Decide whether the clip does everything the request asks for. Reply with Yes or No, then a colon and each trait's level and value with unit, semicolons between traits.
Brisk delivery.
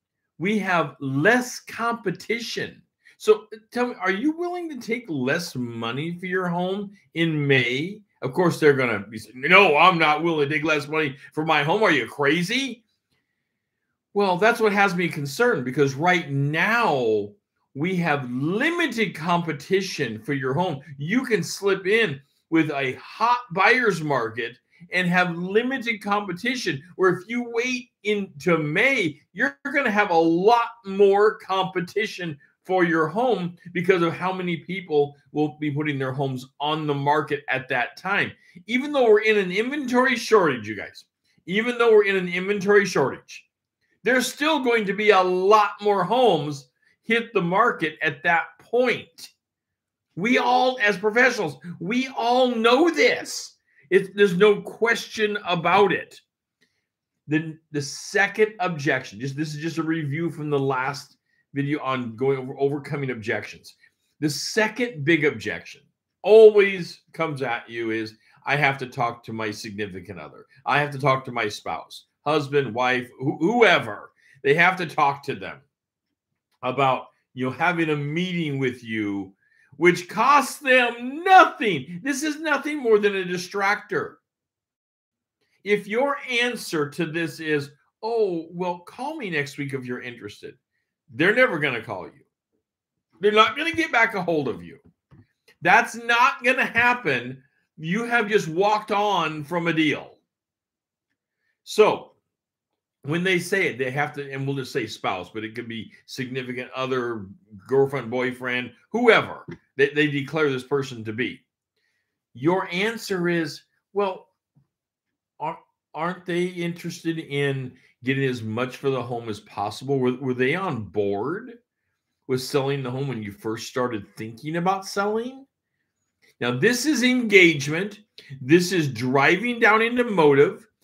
No: average, 155 wpm